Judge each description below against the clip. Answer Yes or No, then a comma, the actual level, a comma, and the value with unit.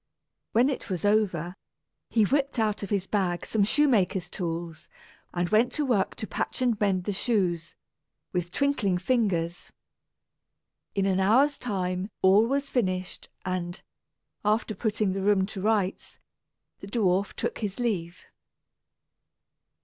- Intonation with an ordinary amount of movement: Yes, average, 3.4 semitones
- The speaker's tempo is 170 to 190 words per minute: No, slow, 135 wpm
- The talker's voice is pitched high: Yes, high, 200 Hz